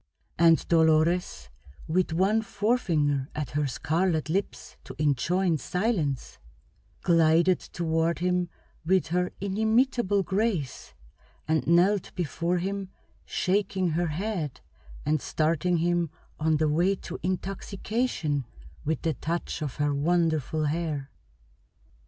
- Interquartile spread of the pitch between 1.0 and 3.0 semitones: No, average, 3.4 semitones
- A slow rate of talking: Yes, slow, 110 wpm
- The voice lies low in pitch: No, medium, 170 Hz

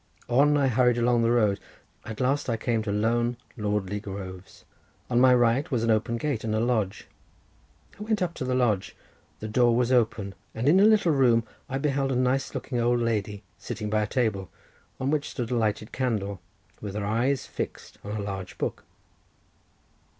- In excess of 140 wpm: Yes, average, 190 wpm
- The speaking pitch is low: Yes, low, 120 Hz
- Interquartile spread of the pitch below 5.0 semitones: Yes, average, 3.4 semitones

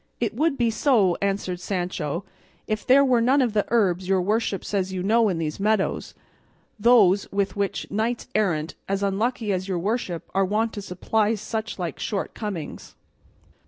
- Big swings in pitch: No, average, 3.2 semitones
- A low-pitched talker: No, high, 205 Hz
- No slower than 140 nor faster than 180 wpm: Yes, average, 165 wpm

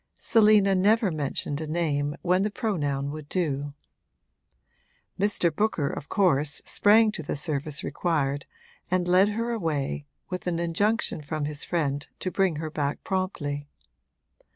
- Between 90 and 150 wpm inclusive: Yes, average, 140 wpm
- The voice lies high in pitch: No, medium, 165 Hz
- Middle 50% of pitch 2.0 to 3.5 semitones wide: No, average, 5.0 semitones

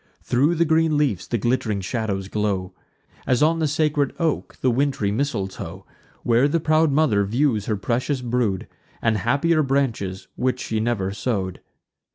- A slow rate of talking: No, average, 155 wpm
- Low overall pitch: Yes, low, 120 Hz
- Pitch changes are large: Yes, wide, 6.2 semitones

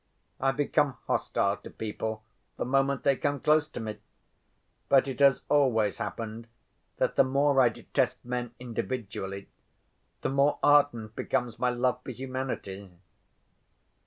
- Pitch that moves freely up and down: No, average, 3.7 semitones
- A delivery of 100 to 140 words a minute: Yes, slow, 135 wpm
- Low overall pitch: Yes, low, 125 Hz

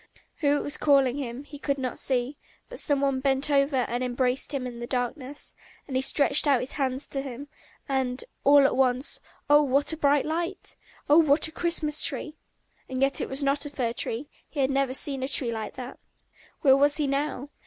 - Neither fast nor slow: No, fast, 215 wpm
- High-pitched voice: Yes, very high, 275 Hz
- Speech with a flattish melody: Yes, narrow, 2.1 semitones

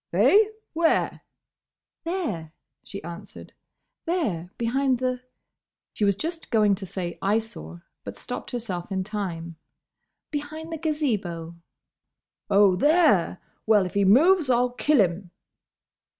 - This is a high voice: Yes, high, 215 Hz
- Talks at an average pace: No, slow, 120 wpm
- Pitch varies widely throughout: Yes, wide, 8.2 semitones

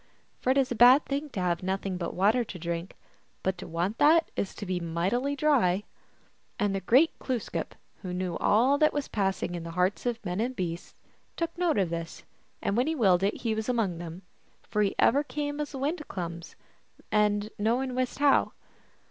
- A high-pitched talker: Yes, high, 210 Hz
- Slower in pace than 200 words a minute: No, fast, 205 wpm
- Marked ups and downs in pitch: Yes, wide, 6.5 semitones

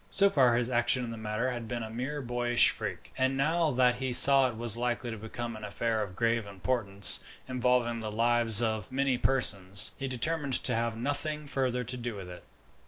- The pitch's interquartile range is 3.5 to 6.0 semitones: No, narrow, 2.5 semitones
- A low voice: Yes, low, 120 Hz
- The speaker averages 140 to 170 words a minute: No, fast, 205 wpm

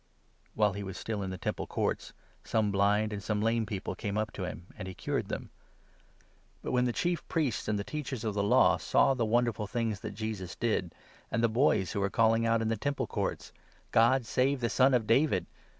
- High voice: No, low, 110 Hz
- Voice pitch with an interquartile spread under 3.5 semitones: Yes, average, 2.8 semitones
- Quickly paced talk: Yes, fast, 235 wpm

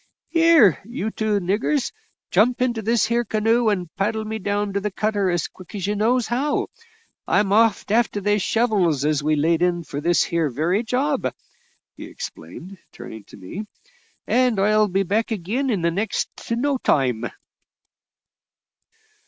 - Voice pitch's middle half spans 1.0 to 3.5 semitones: No, average, 4.6 semitones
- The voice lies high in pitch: Yes, high, 210 Hz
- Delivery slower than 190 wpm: Yes, average, 160 wpm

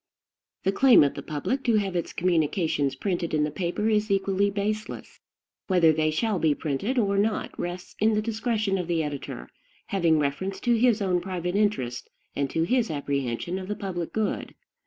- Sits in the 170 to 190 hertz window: Yes, medium, 185 Hz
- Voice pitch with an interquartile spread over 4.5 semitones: Yes, average, 5.0 semitones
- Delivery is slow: No, average, 180 wpm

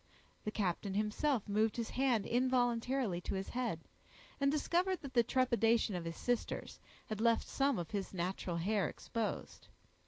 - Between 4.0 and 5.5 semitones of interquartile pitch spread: Yes, average, 4.4 semitones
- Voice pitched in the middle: No, high, 225 Hz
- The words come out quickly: No, average, 155 wpm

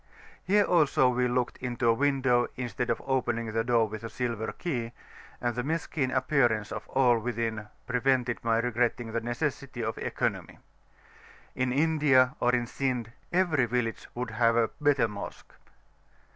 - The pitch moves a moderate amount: No, narrow, 2.3 semitones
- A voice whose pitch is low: Yes, low, 125 Hz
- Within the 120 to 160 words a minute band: Yes, average, 155 wpm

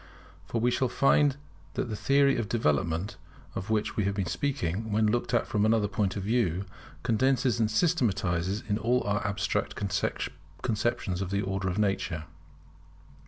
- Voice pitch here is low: Yes, low, 105 Hz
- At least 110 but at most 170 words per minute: Yes, average, 160 wpm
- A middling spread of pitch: Yes, average, 3.7 semitones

